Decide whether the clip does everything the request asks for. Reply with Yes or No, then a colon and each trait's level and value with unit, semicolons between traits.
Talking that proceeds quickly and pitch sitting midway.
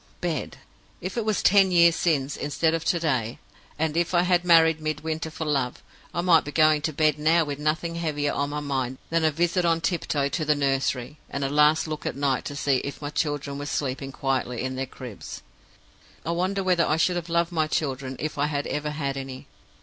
Yes: fast, 220 wpm; medium, 150 Hz